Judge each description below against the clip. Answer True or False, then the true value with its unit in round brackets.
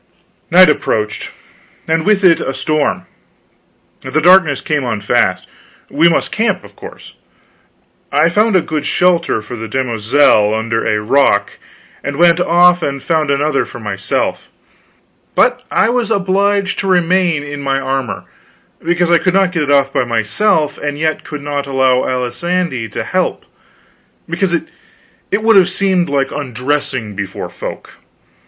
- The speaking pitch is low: False (150 Hz)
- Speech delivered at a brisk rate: False (150 wpm)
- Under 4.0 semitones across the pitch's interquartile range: False (5.3 semitones)